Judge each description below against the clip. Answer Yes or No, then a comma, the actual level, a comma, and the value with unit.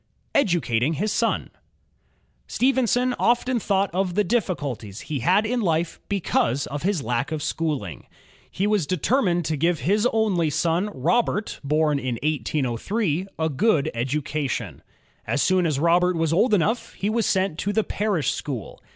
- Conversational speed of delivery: Yes, average, 150 wpm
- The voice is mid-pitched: Yes, medium, 170 Hz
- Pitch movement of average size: No, wide, 6.0 semitones